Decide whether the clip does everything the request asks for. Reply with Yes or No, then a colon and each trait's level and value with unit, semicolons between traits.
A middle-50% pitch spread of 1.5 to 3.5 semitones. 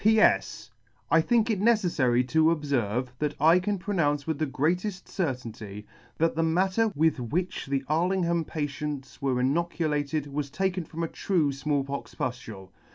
No: average, 4.5 semitones